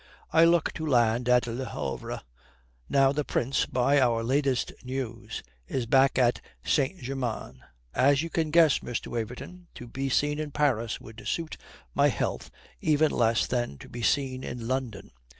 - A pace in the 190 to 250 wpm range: No, average, 165 wpm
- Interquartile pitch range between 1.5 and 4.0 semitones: Yes, average, 3.4 semitones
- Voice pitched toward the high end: No, low, 130 Hz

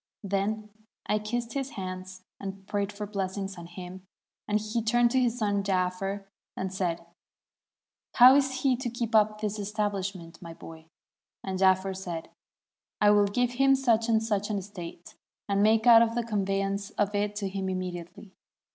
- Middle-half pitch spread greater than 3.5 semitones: No, average, 2.7 semitones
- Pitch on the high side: Yes, high, 205 Hz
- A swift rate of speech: No, average, 175 wpm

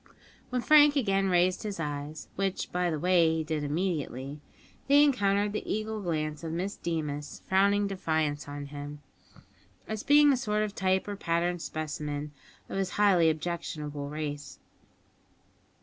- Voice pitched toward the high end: No, medium, 175 Hz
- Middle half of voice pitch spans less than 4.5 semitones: No, average, 5.0 semitones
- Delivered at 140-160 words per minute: Yes, average, 150 wpm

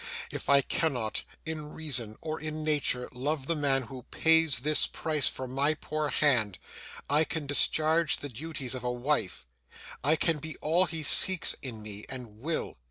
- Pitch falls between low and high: Yes, medium, 145 Hz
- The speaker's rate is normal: Yes, average, 170 wpm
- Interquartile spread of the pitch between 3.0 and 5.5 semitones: Yes, average, 3.8 semitones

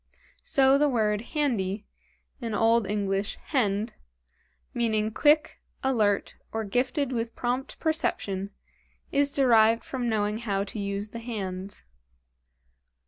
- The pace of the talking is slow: Yes, slow, 115 wpm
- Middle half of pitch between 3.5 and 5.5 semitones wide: Yes, average, 3.8 semitones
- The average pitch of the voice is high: Yes, high, 225 Hz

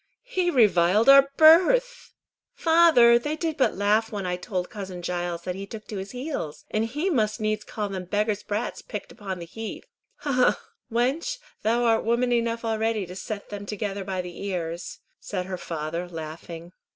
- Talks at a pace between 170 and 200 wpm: Yes, average, 185 wpm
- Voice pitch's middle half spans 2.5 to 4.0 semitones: No, average, 4.9 semitones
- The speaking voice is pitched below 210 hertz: No, high, 215 Hz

